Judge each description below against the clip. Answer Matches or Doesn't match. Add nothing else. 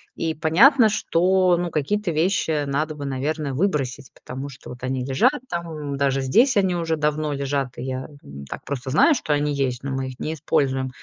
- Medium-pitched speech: Matches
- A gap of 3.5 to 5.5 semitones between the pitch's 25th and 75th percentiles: Matches